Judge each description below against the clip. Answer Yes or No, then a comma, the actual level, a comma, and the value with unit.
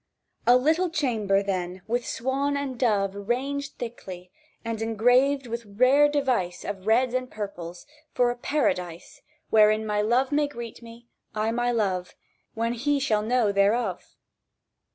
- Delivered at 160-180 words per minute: No, average, 145 wpm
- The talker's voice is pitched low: No, high, 230 Hz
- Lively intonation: No, average, 4.2 semitones